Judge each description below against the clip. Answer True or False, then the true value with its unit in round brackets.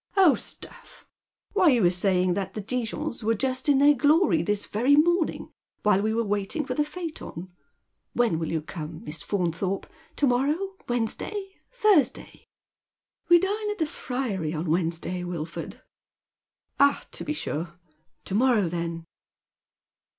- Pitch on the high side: True (225 Hz)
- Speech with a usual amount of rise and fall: False (8.7 semitones)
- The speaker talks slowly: False (165 wpm)